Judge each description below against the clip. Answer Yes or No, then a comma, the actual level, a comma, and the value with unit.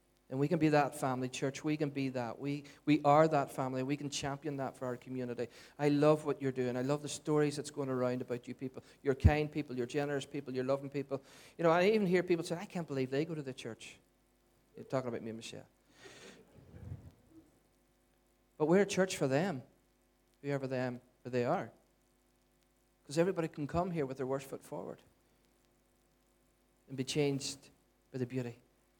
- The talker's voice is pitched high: No, medium, 140 Hz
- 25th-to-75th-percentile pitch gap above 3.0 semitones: No, average, 2.7 semitones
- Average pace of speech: Yes, average, 195 wpm